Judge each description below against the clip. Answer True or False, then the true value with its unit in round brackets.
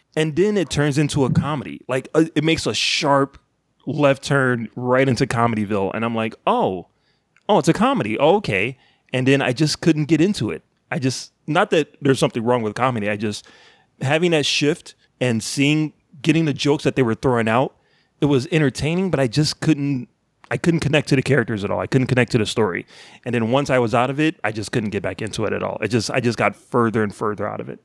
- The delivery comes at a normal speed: False (235 wpm)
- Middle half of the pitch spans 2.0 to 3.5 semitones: False (4.4 semitones)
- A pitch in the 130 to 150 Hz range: True (135 Hz)